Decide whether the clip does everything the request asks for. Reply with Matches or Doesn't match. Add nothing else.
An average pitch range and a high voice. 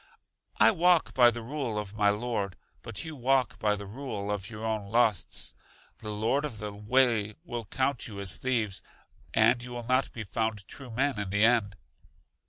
Doesn't match